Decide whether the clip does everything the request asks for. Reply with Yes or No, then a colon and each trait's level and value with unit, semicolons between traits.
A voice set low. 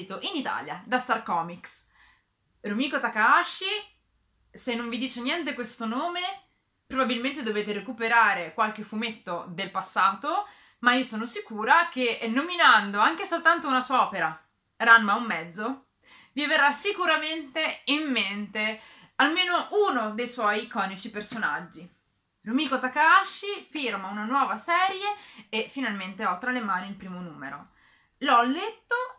No: high, 245 Hz